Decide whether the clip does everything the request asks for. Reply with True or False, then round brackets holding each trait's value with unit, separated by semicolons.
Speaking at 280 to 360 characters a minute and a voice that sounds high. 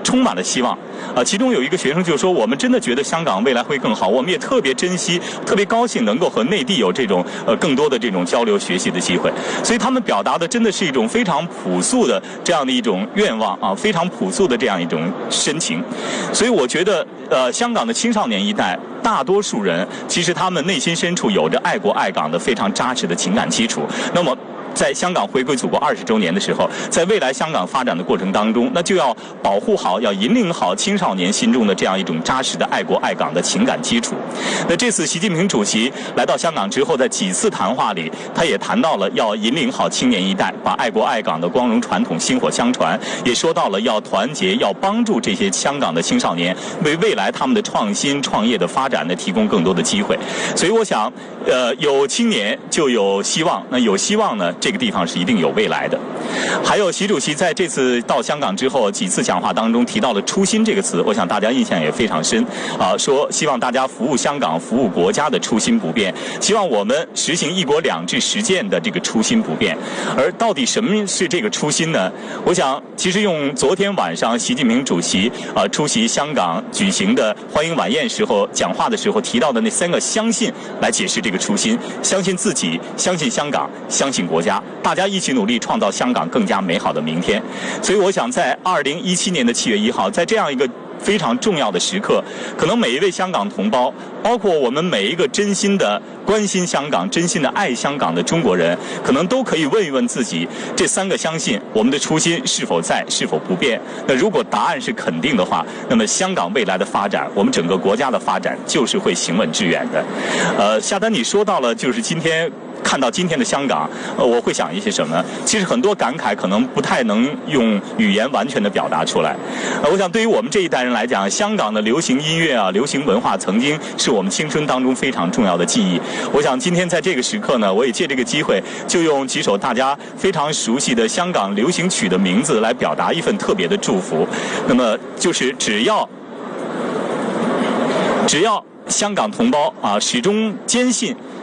True (320 characters per minute; 210 Hz)